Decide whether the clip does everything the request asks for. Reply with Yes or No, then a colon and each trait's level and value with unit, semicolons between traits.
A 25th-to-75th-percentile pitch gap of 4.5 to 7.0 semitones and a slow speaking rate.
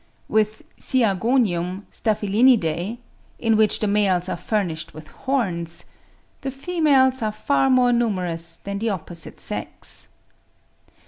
Yes: wide, 5.6 semitones; slow, 115 wpm